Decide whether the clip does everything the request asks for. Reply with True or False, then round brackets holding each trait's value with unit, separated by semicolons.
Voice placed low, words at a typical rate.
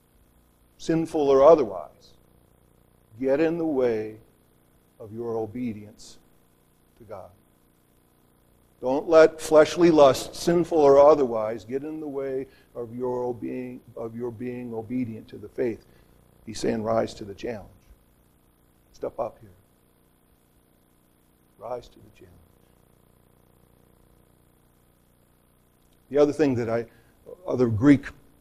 False (120 Hz; 110 wpm)